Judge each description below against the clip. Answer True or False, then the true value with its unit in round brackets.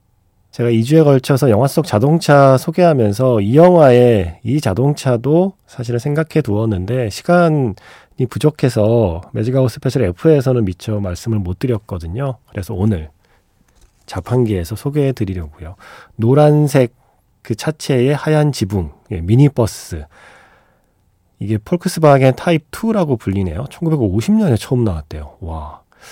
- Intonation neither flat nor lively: False (6.0 semitones)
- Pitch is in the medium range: False (125 Hz)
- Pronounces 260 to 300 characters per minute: True (285 characters per minute)